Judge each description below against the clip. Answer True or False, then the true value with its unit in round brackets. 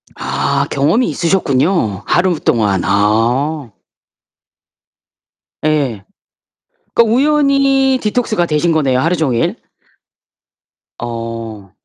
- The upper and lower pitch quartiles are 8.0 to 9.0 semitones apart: True (8.7 semitones)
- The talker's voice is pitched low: False (150 Hz)